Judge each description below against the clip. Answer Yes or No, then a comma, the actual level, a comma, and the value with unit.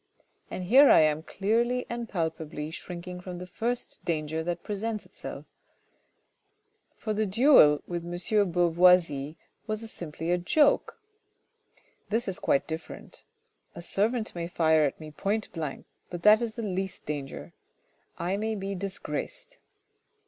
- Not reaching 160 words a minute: Yes, average, 140 wpm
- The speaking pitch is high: No, medium, 180 Hz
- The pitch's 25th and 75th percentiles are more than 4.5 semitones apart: Yes, average, 4.9 semitones